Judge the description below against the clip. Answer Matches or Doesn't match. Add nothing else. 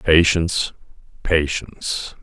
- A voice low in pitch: Matches